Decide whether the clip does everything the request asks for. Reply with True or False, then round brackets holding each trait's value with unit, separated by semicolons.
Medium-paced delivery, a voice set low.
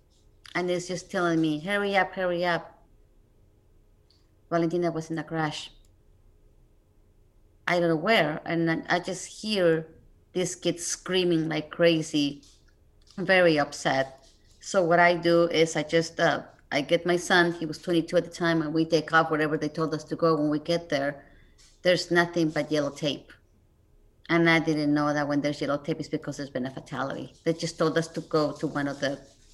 False (185 wpm; 160 Hz)